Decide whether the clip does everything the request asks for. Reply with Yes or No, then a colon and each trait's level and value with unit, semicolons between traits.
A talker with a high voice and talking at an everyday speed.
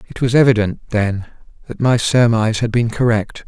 No: low, 115 Hz; average, 175 wpm